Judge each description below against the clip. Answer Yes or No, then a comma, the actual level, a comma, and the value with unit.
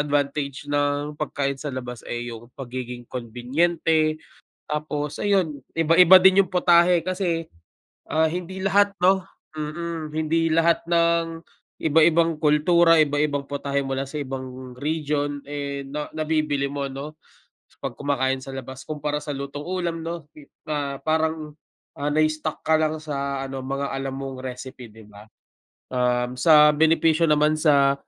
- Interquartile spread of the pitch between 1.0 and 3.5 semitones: Yes, average, 2.9 semitones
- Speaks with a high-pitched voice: No, medium, 150 Hz